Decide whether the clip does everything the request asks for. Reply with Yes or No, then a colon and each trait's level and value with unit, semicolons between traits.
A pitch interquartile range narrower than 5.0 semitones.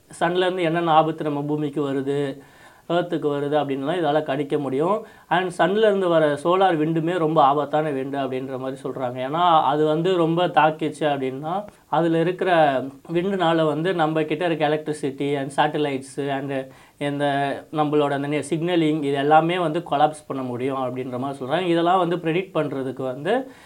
Yes: average, 3.1 semitones